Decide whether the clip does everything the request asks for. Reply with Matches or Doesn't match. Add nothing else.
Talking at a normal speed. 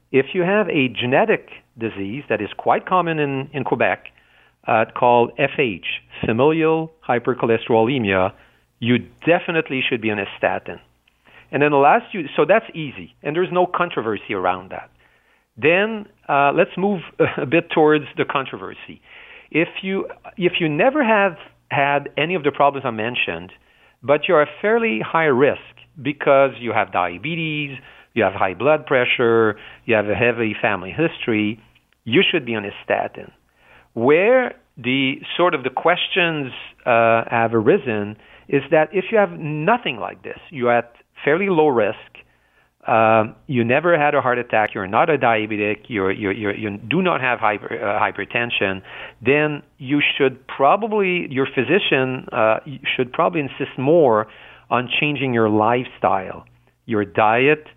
Matches